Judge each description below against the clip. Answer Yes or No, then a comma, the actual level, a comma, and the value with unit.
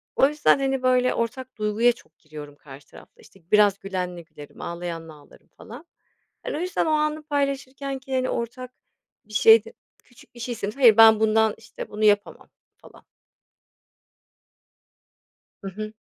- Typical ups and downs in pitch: Yes, average, 4.9 semitones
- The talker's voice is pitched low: No, high, 225 Hz